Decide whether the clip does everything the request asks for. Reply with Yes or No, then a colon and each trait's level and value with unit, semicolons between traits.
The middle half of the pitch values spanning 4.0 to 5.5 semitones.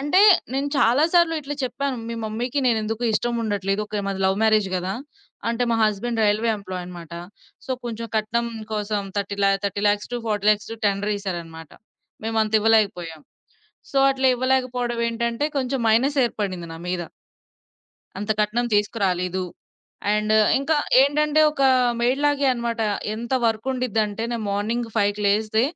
No: average, 3.2 semitones